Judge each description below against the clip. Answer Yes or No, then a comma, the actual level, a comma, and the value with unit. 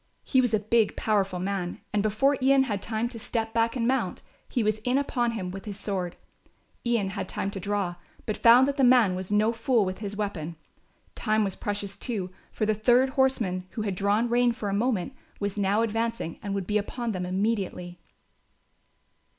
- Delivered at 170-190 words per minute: No, average, 200 wpm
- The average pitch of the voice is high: Yes, high, 215 Hz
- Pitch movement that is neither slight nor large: Yes, average, 3.2 semitones